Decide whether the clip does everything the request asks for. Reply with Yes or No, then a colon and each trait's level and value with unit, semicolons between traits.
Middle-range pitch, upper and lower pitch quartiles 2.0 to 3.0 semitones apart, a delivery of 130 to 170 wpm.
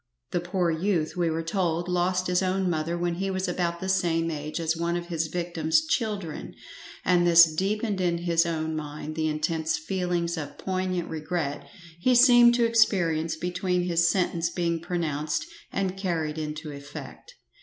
Yes: medium, 170 Hz; narrow, 2.4 semitones; average, 165 wpm